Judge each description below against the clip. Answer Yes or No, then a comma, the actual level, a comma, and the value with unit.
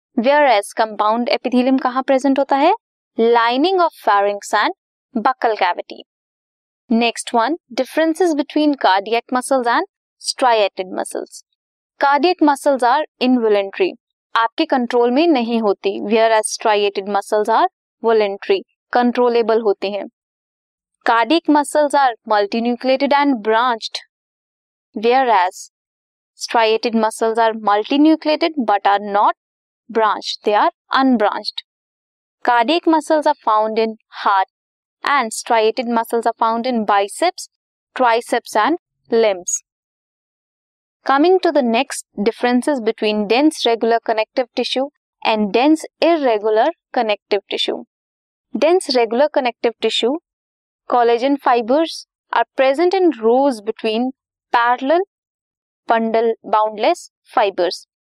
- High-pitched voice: Yes, high, 240 Hz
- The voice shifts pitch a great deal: No, average, 4.5 semitones